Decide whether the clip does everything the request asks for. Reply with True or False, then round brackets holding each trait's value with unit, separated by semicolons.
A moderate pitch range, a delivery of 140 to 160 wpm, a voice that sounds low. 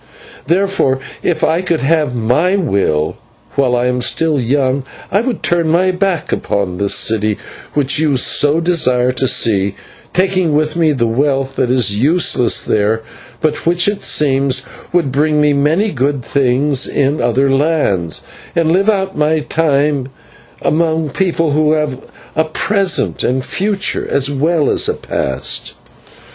False (4.5 semitones; 155 wpm; 145 Hz)